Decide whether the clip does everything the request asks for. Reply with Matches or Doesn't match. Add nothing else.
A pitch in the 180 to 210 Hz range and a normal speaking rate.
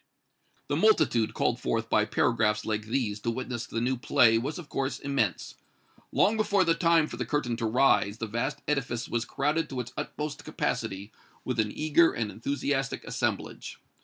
Doesn't match